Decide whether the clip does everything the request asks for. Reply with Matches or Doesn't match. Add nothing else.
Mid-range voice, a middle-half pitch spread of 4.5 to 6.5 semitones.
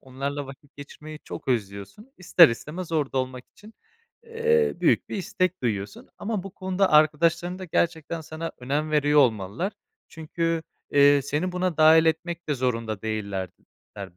Matches